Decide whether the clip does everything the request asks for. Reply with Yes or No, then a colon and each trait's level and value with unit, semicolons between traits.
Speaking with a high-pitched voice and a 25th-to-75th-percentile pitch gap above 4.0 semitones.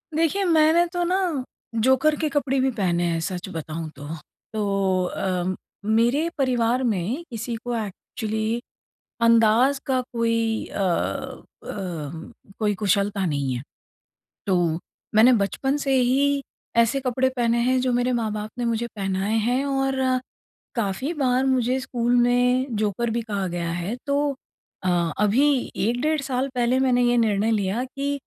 Yes: high, 235 Hz; average, 4.6 semitones